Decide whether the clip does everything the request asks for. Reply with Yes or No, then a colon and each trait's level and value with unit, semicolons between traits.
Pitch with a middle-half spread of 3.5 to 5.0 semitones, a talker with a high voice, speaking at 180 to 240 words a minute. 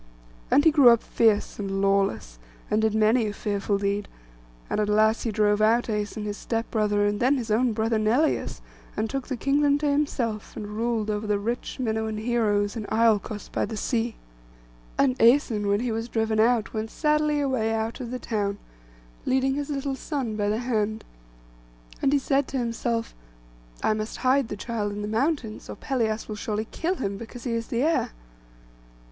No: average, 3.1 semitones; high, 225 Hz; average, 190 wpm